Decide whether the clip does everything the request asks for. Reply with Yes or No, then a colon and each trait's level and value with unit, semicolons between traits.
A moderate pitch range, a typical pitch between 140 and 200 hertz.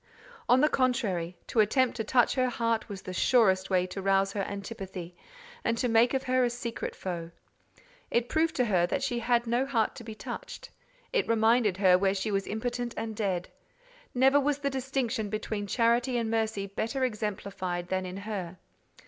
No: average, 4.1 semitones; high, 225 Hz